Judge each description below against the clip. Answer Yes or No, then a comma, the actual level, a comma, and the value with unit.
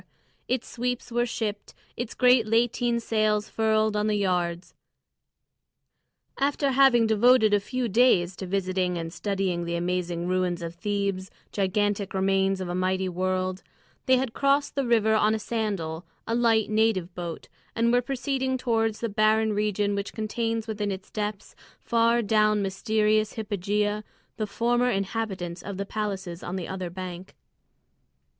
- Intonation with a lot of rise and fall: No, average, 3.5 semitones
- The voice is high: Yes, high, 210 Hz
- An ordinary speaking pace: Yes, average, 150 wpm